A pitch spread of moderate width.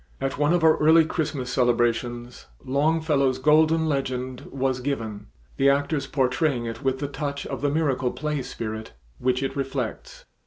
Yes: average, 3.2 semitones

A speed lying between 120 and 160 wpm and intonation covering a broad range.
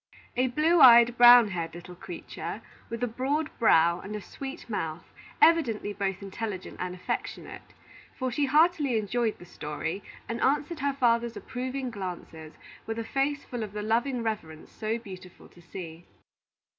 Yes: average, 155 wpm; wide, 5.7 semitones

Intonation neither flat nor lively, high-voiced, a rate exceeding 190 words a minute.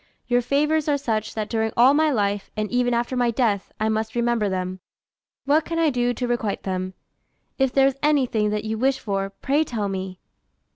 Yes: average, 4.3 semitones; high, 235 Hz; average, 200 wpm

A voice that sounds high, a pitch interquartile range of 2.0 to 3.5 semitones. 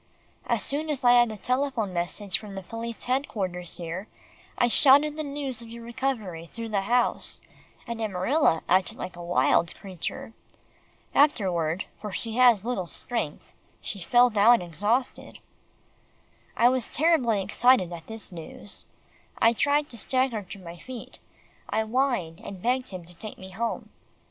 No: high, 225 Hz; average, 5.3 semitones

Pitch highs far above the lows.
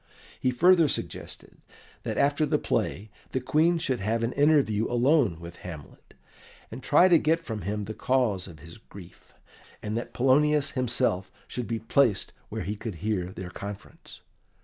Yes: wide, 6.0 semitones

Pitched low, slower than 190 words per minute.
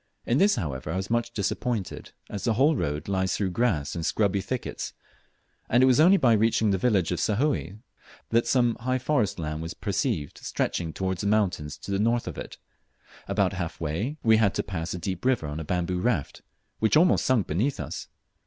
No: low, 100 Hz; average, 200 wpm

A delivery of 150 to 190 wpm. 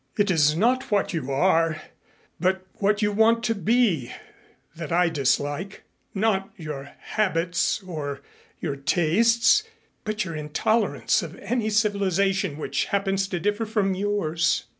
No: slow, 135 wpm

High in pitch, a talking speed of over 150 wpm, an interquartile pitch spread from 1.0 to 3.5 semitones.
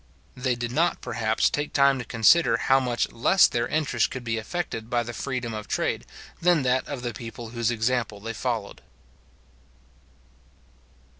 No: low, 120 Hz; average, 160 wpm; narrow, 2.6 semitones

